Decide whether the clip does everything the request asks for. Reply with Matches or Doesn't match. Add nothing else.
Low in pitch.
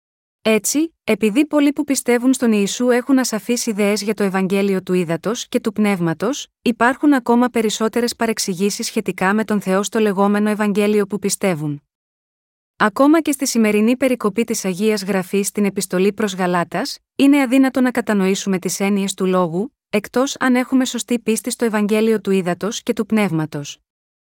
Doesn't match